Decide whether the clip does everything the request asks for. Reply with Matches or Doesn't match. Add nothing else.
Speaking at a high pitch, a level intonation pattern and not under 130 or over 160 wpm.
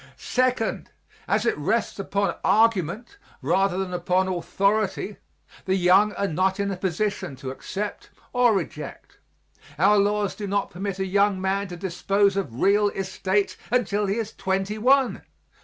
Matches